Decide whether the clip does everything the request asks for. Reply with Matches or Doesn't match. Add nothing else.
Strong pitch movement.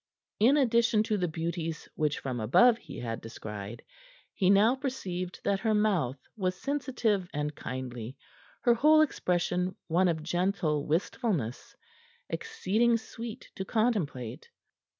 Matches